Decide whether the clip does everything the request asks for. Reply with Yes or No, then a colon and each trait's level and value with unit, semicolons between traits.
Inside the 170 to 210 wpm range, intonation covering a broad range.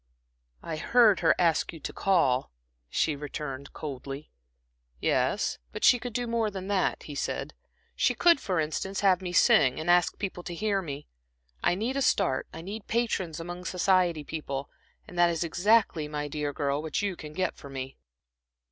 No: average, 175 wpm; average, 4.7 semitones